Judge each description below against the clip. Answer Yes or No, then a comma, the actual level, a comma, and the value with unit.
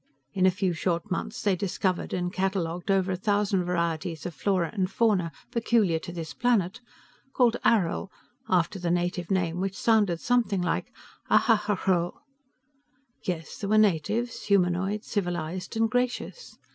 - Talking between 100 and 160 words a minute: Yes, average, 145 wpm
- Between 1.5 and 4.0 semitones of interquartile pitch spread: Yes, average, 3.2 semitones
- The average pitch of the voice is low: No, medium, 185 Hz